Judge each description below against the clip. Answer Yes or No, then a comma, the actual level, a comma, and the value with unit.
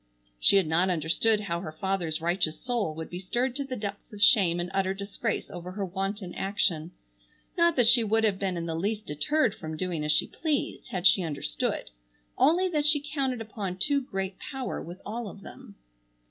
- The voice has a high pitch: Yes, high, 195 Hz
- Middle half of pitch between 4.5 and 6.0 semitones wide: Yes, average, 5.3 semitones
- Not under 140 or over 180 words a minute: No, average, 200 wpm